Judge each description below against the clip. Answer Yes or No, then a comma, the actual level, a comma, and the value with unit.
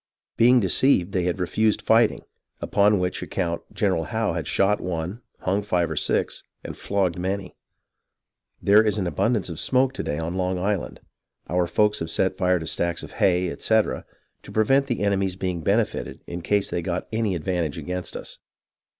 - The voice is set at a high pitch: No, very low, 95 Hz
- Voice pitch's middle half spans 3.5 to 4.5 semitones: No, average, 3.1 semitones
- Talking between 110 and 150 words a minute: No, average, 175 wpm